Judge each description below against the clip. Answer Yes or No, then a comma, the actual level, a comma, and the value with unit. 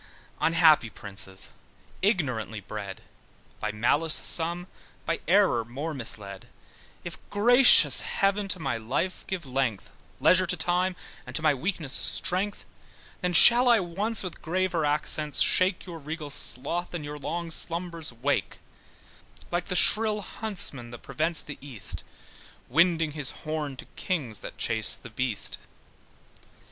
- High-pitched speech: No, medium, 160 Hz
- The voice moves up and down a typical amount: No, wide, 6.0 semitones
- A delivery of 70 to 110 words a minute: No, slow, 135 wpm